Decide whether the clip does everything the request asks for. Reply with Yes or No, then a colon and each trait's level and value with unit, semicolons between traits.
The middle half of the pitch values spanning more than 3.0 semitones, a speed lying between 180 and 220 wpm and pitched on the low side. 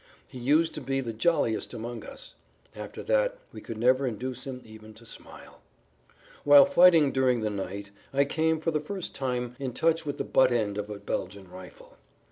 Yes: wide, 5.6 semitones; average, 190 wpm; low, 130 Hz